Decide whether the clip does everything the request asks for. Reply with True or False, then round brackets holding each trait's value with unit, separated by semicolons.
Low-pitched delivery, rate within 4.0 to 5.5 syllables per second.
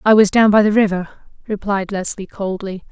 False (200 Hz; 5.0 syllables/s)